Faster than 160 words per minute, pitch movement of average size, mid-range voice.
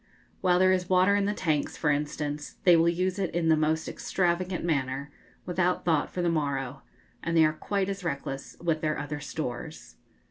Yes: average, 190 wpm; average, 3.6 semitones; medium, 165 Hz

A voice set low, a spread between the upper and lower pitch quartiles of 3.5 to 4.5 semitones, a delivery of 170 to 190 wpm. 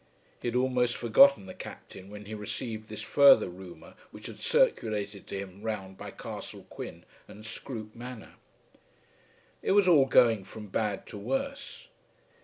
No: low, 110 Hz; average, 4.1 semitones; average, 155 wpm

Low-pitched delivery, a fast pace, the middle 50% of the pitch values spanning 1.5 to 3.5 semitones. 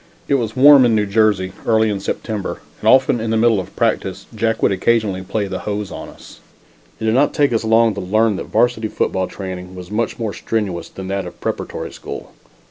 Yes: low, 110 Hz; fast, 215 wpm; average, 2.9 semitones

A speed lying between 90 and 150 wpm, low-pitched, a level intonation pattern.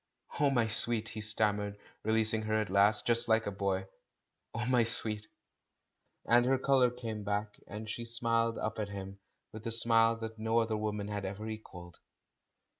No: average, 190 wpm; low, 110 Hz; narrow, 1.8 semitones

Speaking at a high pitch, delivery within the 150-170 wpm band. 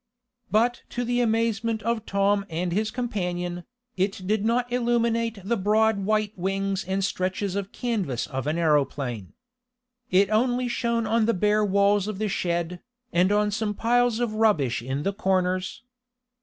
Yes: high, 205 Hz; average, 155 wpm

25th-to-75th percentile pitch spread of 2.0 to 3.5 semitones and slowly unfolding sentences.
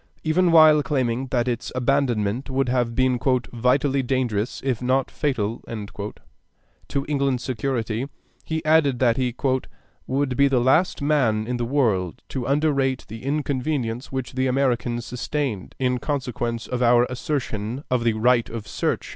No: average, 2.7 semitones; average, 145 wpm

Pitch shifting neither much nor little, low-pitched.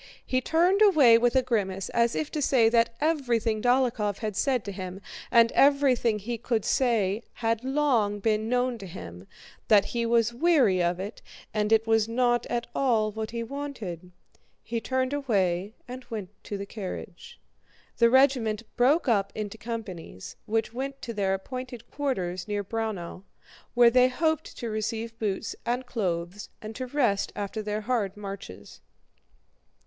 No: average, 3.7 semitones; high, 230 Hz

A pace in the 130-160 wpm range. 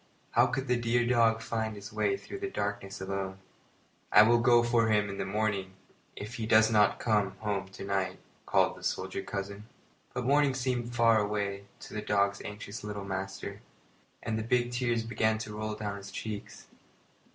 No: average, 185 wpm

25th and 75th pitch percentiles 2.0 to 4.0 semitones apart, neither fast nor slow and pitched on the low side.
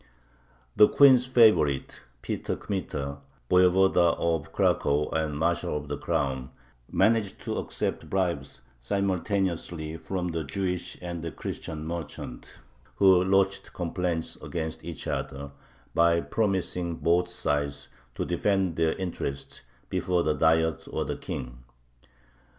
No: average, 3.7 semitones; slow, 120 wpm; very low, 85 Hz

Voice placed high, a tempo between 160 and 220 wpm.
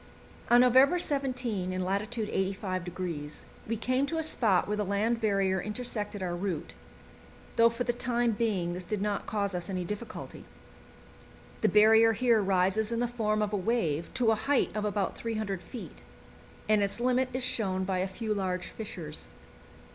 Yes: high, 210 Hz; average, 170 wpm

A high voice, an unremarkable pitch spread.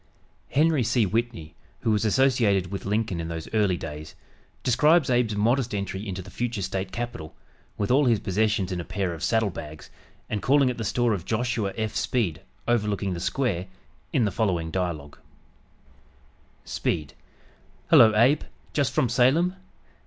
No: low, 105 Hz; average, 4.6 semitones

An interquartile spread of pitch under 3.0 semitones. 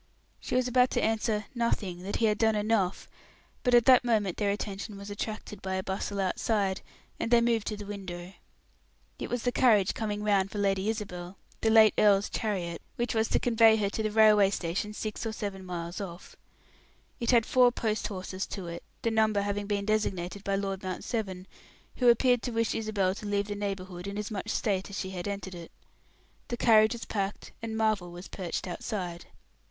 Yes: narrow, 2.6 semitones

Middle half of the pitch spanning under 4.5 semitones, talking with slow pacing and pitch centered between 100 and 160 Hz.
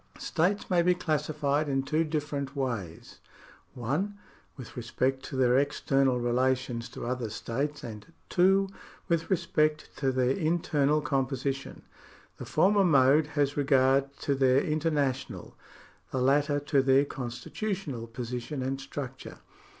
Yes: average, 2.9 semitones; slow, 130 wpm; medium, 140 Hz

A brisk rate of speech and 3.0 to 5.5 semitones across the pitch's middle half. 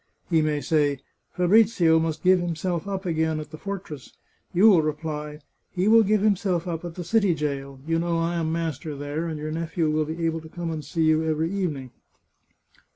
No: fast, 220 wpm; narrow, 2.5 semitones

